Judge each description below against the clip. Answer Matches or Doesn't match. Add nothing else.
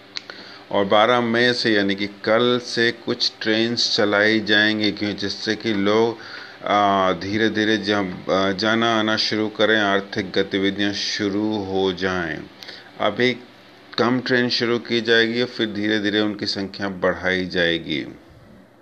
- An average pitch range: Doesn't match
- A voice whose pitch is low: Matches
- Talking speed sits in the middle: Matches